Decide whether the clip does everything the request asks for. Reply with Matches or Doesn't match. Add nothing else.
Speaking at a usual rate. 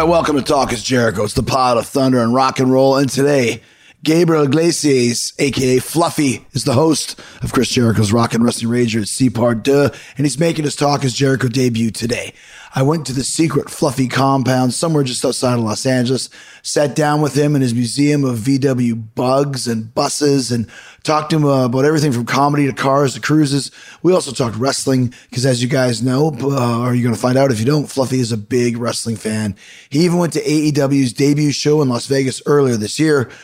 Doesn't match